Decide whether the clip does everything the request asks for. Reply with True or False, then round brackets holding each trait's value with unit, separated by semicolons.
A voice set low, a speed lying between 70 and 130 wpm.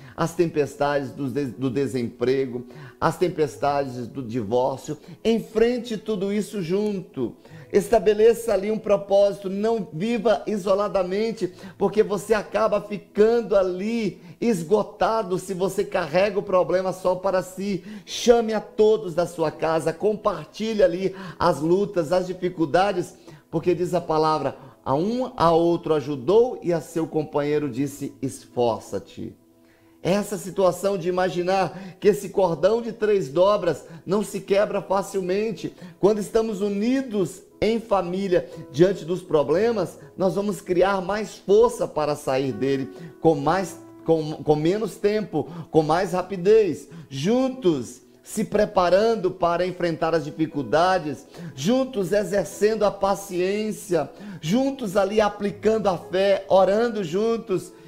False (185 Hz; 125 wpm)